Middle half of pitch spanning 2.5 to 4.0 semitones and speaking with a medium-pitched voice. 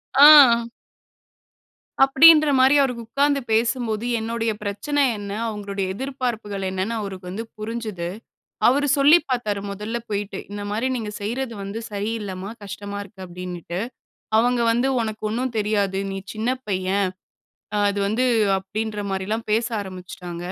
No: average, 3.3 semitones; high, 215 Hz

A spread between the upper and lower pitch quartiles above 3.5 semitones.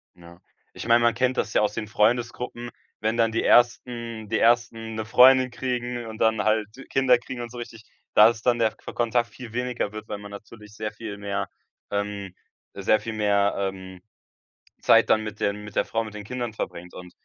No: narrow, 2.5 semitones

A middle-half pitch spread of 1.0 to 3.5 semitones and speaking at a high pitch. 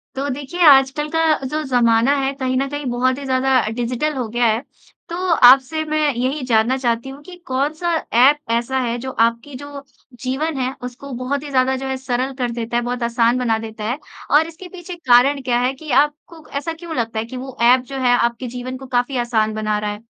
Yes: average, 2.8 semitones; very high, 260 Hz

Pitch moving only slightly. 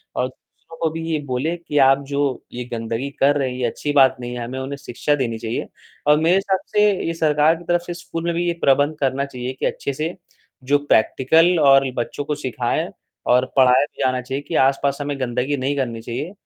No: average, 3.6 semitones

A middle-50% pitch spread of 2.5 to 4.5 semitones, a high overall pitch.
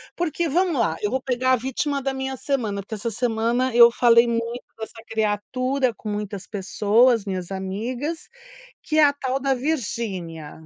Yes: average, 4.0 semitones; high, 235 Hz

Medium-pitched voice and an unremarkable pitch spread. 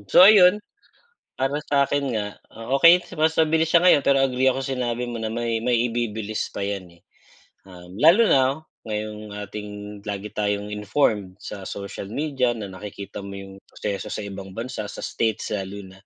No: low, 110 Hz; average, 4.9 semitones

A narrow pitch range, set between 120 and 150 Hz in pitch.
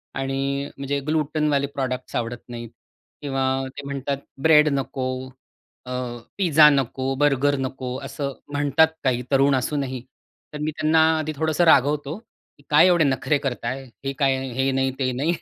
Yes: narrow, 2.0 semitones; medium, 140 Hz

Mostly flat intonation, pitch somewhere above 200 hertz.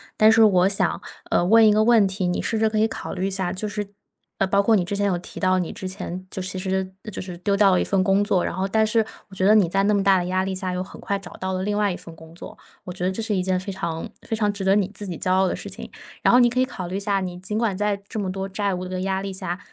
No: narrow, 1.9 semitones; high, 195 Hz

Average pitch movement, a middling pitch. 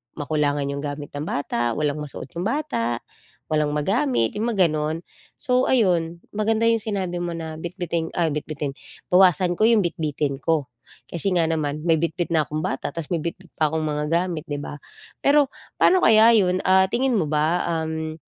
Yes: average, 3.8 semitones; medium, 165 Hz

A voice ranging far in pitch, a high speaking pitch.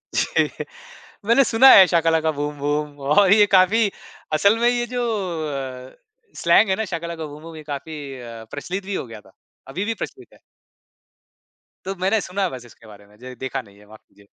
No: wide, 6.8 semitones; medium, 160 Hz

